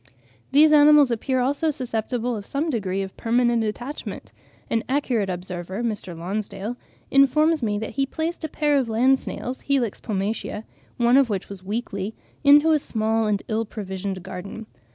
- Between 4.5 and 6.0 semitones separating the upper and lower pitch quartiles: Yes, average, 5.2 semitones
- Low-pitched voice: No, high, 230 Hz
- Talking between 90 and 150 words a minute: No, average, 160 wpm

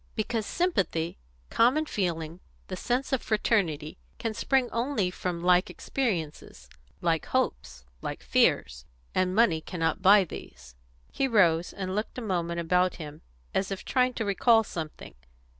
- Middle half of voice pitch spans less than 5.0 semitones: No, wide, 5.6 semitones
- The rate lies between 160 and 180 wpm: No, average, 140 wpm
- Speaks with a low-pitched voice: No, medium, 185 Hz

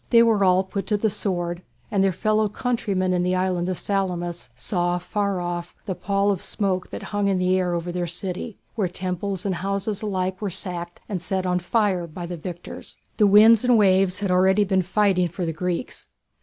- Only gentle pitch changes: Yes, narrow, 2.2 semitones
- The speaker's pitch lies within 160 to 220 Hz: Yes, medium, 185 Hz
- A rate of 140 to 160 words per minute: No, average, 195 wpm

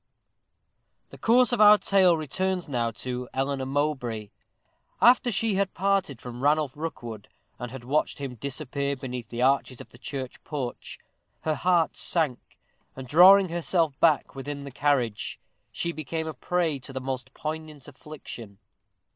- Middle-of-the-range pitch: Yes, medium, 145 Hz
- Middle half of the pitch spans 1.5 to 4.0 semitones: No, average, 4.7 semitones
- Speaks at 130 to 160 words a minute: Yes, average, 155 wpm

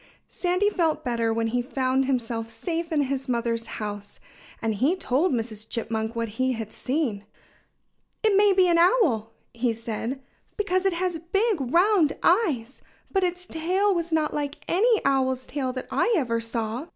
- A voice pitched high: Yes, very high, 270 Hz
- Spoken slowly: No, average, 165 wpm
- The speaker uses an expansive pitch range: Yes, wide, 7.4 semitones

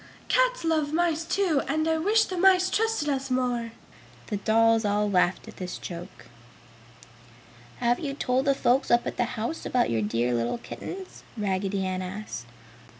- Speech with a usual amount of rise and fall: No, wide, 8.4 semitones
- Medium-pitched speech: No, high, 245 Hz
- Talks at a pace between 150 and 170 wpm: Yes, average, 165 wpm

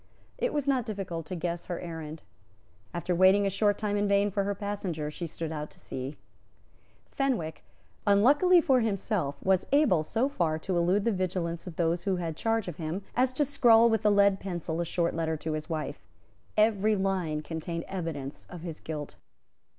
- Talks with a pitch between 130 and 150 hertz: No, medium, 185 Hz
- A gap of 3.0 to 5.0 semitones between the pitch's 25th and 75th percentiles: Yes, average, 4.3 semitones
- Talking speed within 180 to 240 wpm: Yes, average, 190 wpm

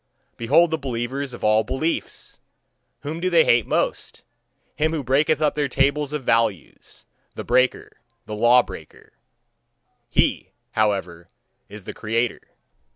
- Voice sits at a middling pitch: No, low, 130 Hz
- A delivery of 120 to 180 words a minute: Yes, slow, 135 wpm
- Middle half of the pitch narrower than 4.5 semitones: No, average, 4.8 semitones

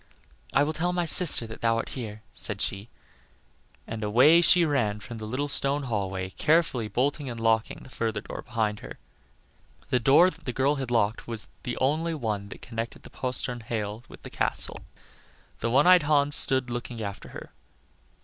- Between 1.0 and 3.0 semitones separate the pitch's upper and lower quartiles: No, average, 4.7 semitones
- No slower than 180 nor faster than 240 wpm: Yes, average, 185 wpm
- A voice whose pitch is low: Yes, low, 120 Hz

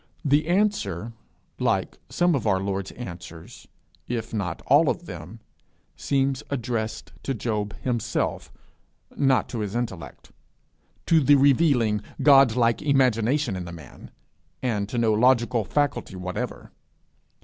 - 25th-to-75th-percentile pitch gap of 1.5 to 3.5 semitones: No, average, 4.9 semitones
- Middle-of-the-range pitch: No, low, 120 Hz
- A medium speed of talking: No, slow, 125 wpm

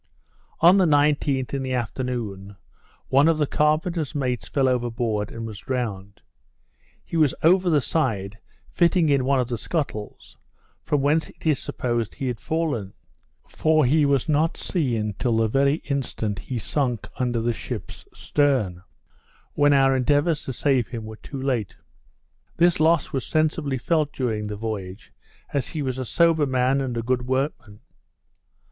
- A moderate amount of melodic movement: Yes, average, 4.5 semitones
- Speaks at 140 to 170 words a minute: Yes, average, 160 wpm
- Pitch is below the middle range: Yes, low, 130 Hz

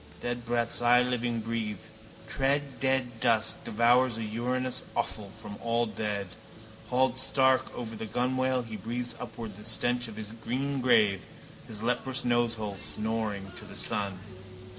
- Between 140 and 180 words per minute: Yes, average, 145 wpm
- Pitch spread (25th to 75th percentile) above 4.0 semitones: No, narrow, 2.5 semitones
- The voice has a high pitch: No, low, 120 Hz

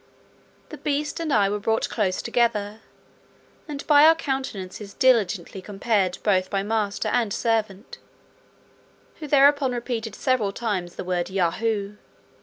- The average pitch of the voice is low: No, high, 220 Hz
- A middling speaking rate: No, slow, 130 wpm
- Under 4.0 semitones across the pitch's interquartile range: No, average, 4.6 semitones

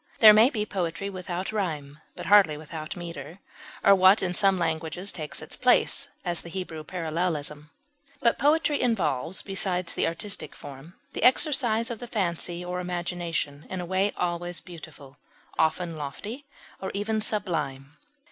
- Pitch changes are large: No, average, 4.1 semitones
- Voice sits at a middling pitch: Yes, medium, 180 Hz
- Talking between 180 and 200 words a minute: No, average, 150 wpm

